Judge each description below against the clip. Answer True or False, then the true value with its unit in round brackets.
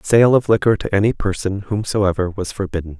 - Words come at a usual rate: True (180 wpm)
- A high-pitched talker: False (100 Hz)